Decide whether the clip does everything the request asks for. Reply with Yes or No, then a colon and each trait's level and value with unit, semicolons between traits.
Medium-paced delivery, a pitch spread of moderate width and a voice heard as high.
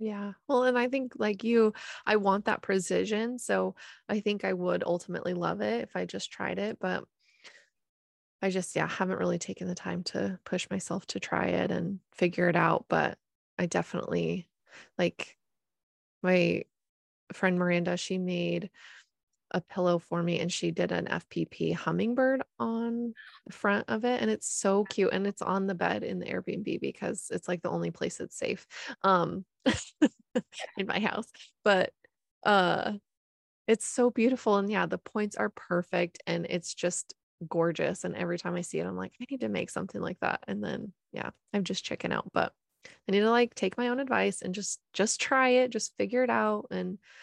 Yes: average, 185 wpm; average, 3.9 semitones; high, 195 Hz